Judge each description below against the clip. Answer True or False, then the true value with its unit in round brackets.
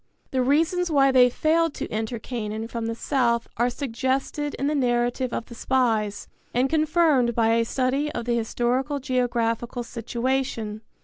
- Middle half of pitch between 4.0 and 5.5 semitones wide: False (2.8 semitones)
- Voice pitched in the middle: False (250 Hz)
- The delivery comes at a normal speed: True (160 wpm)